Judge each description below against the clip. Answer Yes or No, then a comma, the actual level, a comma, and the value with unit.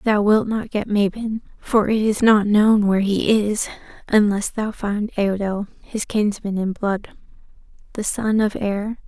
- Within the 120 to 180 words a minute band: Yes, average, 165 wpm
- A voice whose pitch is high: Yes, high, 210 Hz